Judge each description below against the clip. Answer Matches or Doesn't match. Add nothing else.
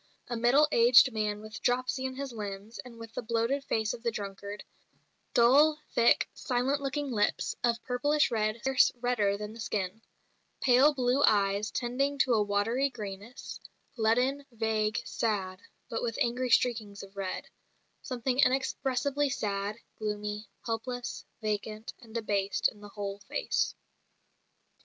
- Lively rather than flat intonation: Doesn't match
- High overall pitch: Matches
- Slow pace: Doesn't match